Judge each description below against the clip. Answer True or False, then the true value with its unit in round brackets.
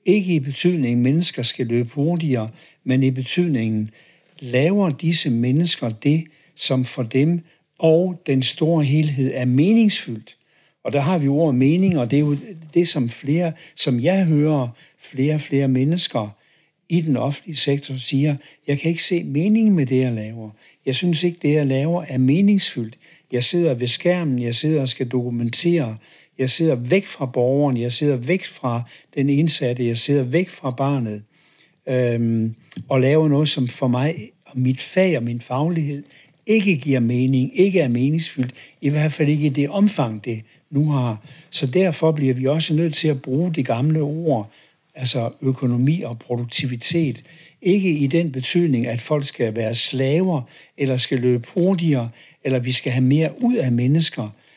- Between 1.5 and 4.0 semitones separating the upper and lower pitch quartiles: False (4.4 semitones)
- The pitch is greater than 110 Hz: True (140 Hz)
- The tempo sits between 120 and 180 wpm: True (175 wpm)